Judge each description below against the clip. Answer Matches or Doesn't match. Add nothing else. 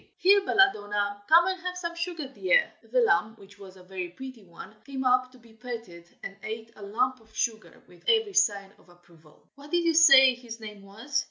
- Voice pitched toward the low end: Doesn't match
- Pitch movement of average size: Doesn't match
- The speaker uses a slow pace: Doesn't match